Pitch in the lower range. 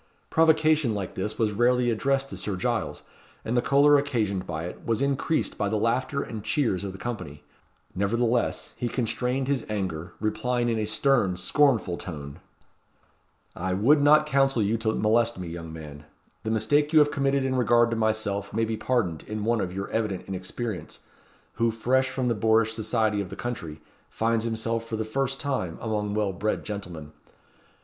Yes: low, 110 Hz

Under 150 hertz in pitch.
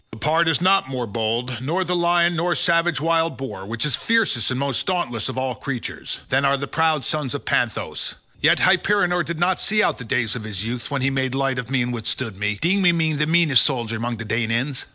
Yes: low, 135 Hz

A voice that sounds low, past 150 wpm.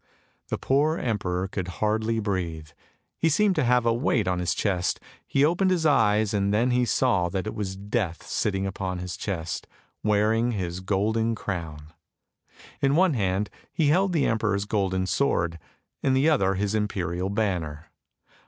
Yes: low, 105 Hz; average, 165 wpm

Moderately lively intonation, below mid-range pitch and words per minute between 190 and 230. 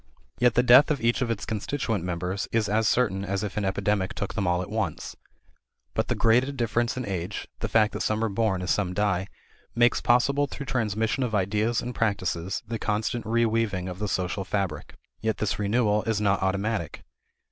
Yes: average, 3.2 semitones; low, 105 Hz; average, 195 wpm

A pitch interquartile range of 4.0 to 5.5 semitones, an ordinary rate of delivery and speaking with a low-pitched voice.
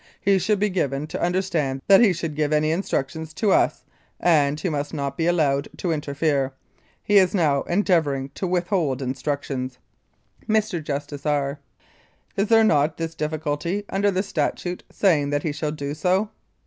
No: average, 4.4 semitones; average, 170 wpm; medium, 155 Hz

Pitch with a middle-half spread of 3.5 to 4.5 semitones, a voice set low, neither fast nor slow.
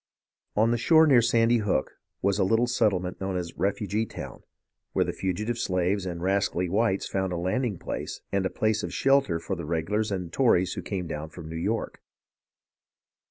Yes: average, 3.9 semitones; low, 100 Hz; average, 185 wpm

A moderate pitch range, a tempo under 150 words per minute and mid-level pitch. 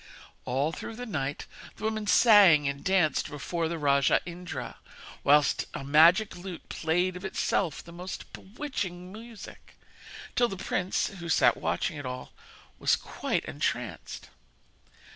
Yes: average, 4.6 semitones; average, 140 wpm; medium, 175 Hz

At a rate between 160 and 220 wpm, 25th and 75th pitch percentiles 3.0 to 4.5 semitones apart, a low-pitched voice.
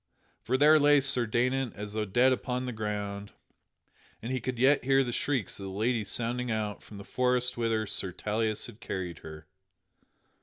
Yes: average, 185 wpm; average, 3.5 semitones; low, 115 Hz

